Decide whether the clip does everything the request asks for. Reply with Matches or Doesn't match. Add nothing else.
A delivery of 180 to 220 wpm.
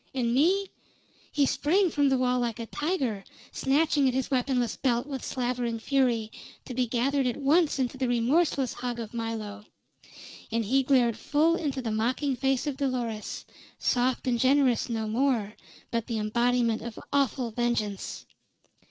Doesn't match